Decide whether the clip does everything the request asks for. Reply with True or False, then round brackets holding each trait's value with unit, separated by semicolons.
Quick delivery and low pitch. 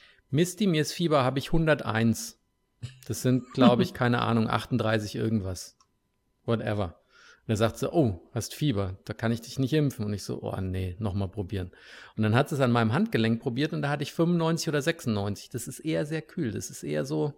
True (210 wpm; 115 Hz)